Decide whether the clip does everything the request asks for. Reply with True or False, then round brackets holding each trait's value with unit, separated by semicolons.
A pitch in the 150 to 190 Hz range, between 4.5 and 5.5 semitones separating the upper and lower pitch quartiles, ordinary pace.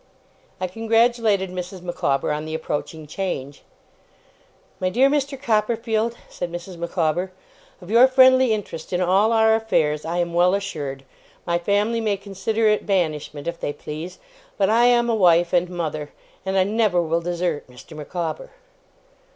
True (185 Hz; 4.8 semitones; 155 wpm)